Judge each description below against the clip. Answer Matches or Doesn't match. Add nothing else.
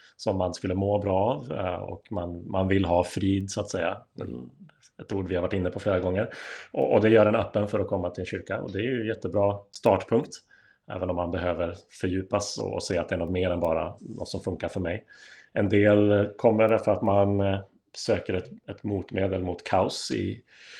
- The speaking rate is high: Matches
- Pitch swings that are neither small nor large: Doesn't match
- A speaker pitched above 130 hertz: Doesn't match